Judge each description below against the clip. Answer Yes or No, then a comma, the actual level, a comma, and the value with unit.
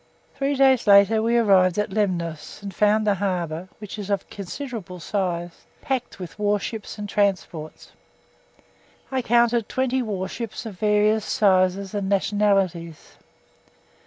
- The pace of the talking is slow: Yes, slow, 130 wpm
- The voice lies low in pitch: No, high, 205 Hz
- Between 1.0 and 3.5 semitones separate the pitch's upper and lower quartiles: Yes, average, 3.0 semitones